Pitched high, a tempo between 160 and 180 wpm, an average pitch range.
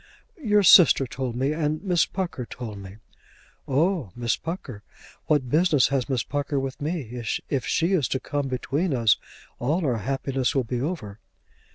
No: low, 135 Hz; average, 165 wpm; average, 4.5 semitones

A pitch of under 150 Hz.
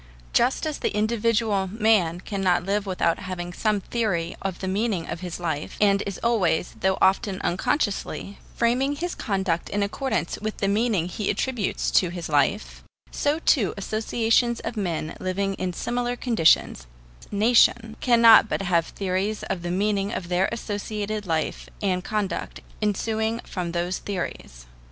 No: high, 200 Hz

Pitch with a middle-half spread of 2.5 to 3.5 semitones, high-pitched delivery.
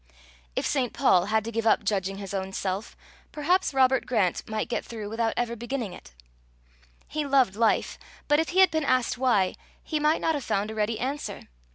No: average, 5.0 semitones; high, 235 Hz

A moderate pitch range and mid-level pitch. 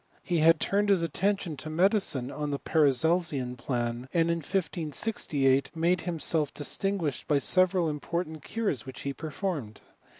Yes: average, 4.4 semitones; medium, 160 Hz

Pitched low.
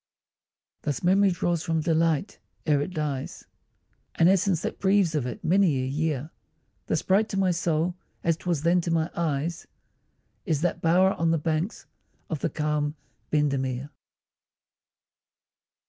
No: medium, 165 Hz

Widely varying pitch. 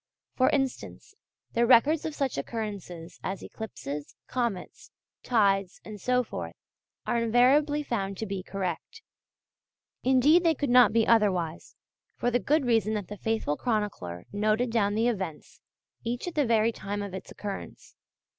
No: average, 4.1 semitones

